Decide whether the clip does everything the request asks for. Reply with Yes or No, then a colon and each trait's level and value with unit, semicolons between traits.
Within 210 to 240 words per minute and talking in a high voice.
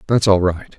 No: fast, 230 wpm; low, 100 Hz